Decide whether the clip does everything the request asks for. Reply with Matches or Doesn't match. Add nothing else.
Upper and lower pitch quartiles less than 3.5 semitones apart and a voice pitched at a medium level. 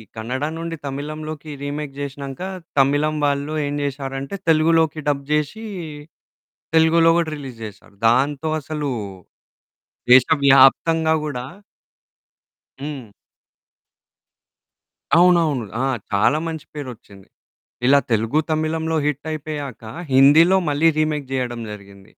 Matches